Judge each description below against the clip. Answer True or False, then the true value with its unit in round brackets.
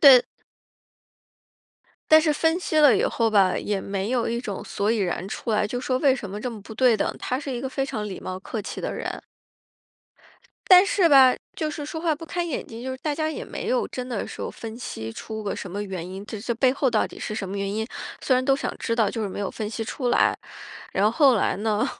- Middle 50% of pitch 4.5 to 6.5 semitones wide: True (4.9 semitones)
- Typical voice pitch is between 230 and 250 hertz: True (235 Hz)